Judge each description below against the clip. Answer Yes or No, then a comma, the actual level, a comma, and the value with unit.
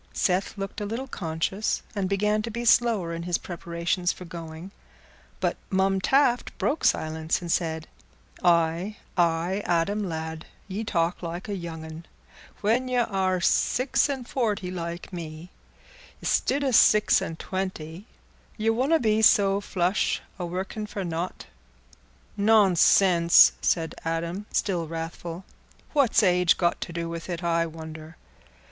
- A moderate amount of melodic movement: Yes, average, 3.9 semitones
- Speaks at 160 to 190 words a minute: No, average, 140 wpm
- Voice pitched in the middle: Yes, medium, 180 Hz